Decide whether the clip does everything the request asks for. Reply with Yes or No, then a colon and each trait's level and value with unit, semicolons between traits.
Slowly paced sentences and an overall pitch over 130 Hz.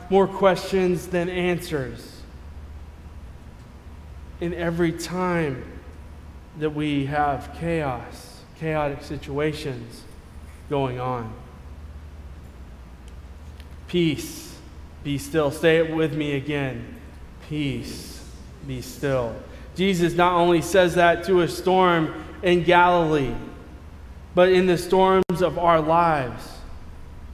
Yes: slow, 95 wpm; medium, 140 Hz